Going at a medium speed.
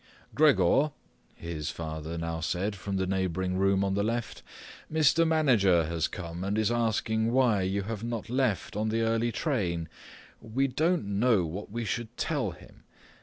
Yes: average, 165 wpm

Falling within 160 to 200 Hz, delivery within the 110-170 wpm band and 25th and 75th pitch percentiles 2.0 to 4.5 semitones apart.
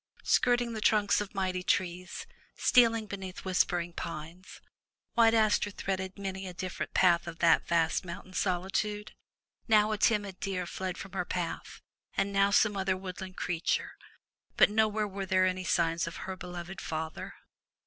Yes: high, 190 Hz; average, 155 wpm; narrow, 2.6 semitones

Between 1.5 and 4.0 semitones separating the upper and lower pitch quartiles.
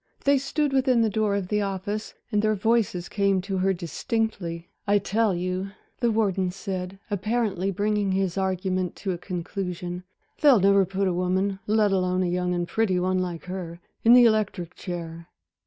Yes: average, 2.8 semitones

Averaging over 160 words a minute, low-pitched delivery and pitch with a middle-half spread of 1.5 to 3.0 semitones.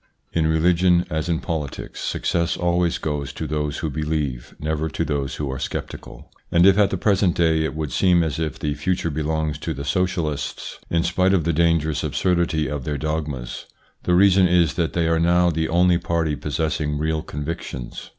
Yes: average, 190 wpm; very low, 80 Hz; narrow, 2.5 semitones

